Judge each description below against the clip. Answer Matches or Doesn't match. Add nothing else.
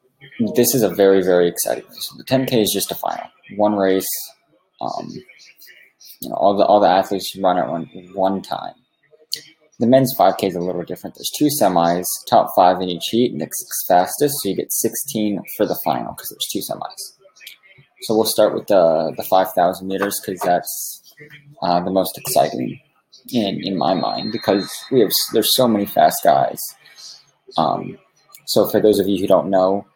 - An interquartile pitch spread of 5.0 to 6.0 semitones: Matches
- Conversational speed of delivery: Matches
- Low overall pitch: Matches